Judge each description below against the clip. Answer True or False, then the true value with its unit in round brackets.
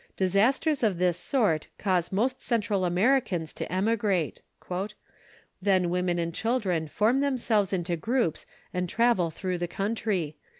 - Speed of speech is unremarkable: False (130 wpm)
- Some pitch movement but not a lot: True (4.7 semitones)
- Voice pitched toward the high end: True (195 Hz)